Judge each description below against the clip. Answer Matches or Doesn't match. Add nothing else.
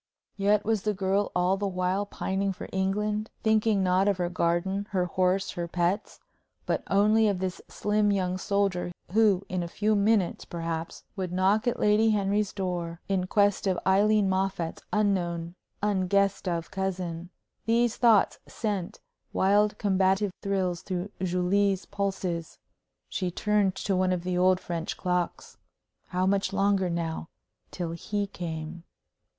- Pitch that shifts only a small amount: Matches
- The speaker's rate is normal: Matches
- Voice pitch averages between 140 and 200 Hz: Matches